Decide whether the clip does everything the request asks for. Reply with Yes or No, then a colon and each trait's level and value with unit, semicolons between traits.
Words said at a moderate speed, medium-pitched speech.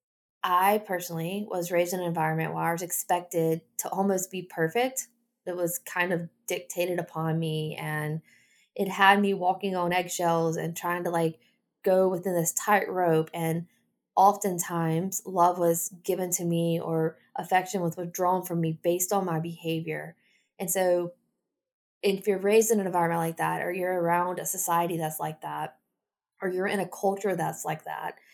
Yes: average, 170 wpm; medium, 175 Hz